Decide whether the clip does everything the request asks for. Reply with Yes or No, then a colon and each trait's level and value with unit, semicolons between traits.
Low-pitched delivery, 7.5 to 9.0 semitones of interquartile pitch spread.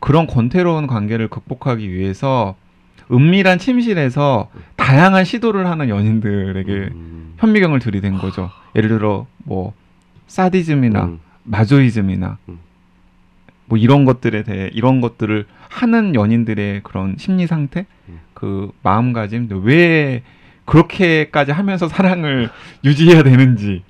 Yes: low, 120 Hz; wide, 7.9 semitones